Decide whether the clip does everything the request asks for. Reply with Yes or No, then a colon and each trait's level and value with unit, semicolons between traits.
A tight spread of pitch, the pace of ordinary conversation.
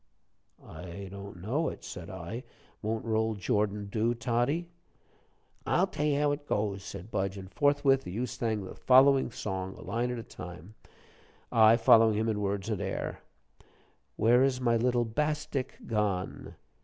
No: average, 4.1 semitones; average, 160 wpm